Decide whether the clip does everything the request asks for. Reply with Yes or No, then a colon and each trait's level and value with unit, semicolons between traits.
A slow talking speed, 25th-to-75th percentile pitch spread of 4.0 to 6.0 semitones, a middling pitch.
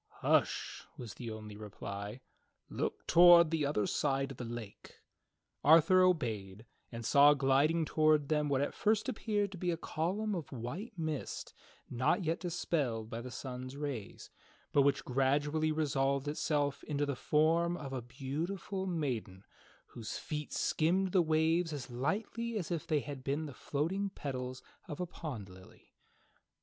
No: average, 155 wpm; average, 4.7 semitones; medium, 145 Hz